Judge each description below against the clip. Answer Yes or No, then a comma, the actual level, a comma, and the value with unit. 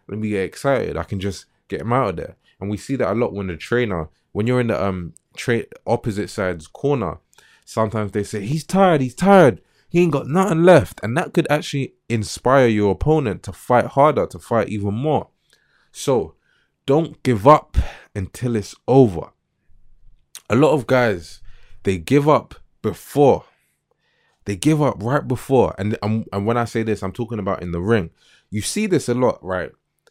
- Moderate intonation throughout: No, wide, 5.7 semitones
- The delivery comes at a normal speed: Yes, average, 190 wpm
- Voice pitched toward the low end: Yes, low, 115 Hz